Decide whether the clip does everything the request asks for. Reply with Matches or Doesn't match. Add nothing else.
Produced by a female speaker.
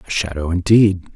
Doesn't match